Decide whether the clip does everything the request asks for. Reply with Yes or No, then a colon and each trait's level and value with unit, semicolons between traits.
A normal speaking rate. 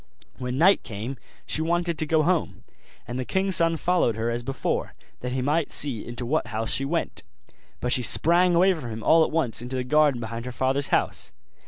No: fast, 210 wpm